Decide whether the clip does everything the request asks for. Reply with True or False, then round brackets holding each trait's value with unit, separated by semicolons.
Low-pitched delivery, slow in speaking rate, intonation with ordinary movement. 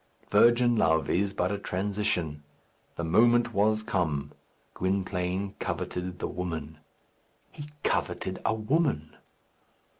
True (95 Hz; 110 wpm; 3.7 semitones)